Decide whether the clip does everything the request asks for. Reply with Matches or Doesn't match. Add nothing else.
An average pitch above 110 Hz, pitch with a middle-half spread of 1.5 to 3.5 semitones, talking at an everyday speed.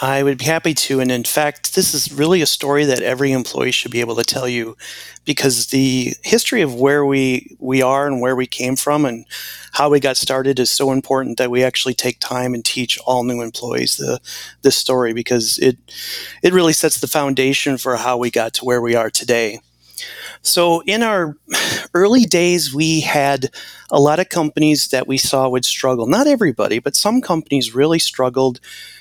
Matches